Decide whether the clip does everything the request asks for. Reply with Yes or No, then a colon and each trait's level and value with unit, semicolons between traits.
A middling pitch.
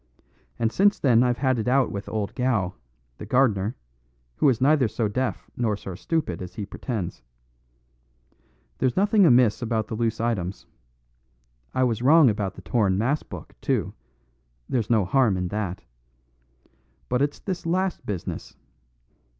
No: low, 120 Hz